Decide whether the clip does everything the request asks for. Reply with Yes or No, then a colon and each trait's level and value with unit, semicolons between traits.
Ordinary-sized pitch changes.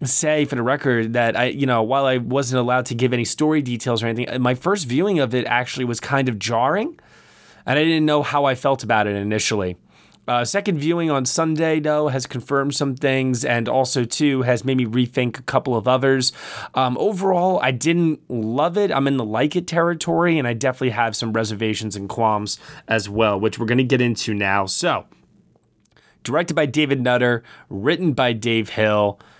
Yes: average, 4.2 semitones